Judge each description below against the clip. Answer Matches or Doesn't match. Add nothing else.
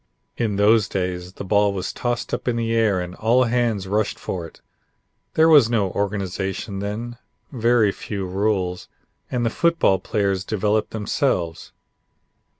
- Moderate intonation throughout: Matches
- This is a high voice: Doesn't match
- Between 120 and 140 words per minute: Doesn't match